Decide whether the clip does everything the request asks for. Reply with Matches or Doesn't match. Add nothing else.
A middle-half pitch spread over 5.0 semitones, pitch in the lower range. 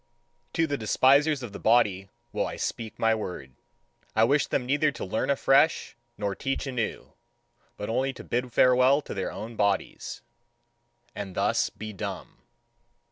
Doesn't match